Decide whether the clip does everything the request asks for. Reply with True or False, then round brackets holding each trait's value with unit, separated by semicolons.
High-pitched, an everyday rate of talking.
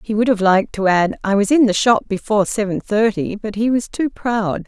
False (210 Hz; 245 wpm)